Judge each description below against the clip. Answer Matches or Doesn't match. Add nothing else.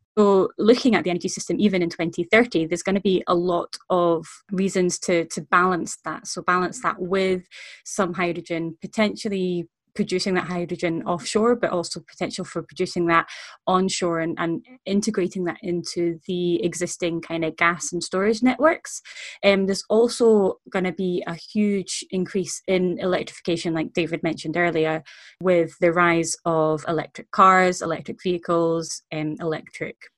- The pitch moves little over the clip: Matches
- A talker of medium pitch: Matches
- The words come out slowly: Doesn't match